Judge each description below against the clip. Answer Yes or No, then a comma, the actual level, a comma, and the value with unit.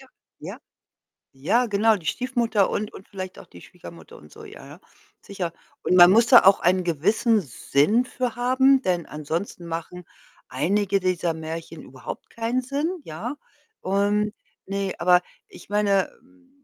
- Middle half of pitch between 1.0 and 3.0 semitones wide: No, average, 5.3 semitones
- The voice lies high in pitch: Yes, high, 200 Hz